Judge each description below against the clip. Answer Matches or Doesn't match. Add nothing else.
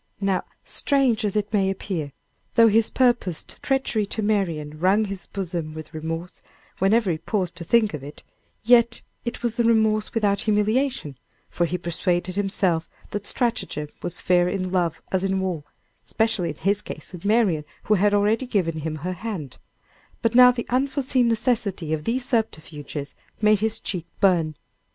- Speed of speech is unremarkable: Matches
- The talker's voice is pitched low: Doesn't match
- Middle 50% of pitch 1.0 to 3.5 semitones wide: Doesn't match